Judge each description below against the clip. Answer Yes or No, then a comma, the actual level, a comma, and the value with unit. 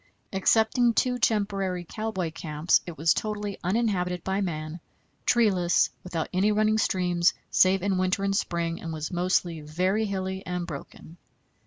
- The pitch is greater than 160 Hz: Yes, medium, 185 Hz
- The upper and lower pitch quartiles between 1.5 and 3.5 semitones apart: Yes, average, 3.2 semitones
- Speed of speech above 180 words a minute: No, average, 145 wpm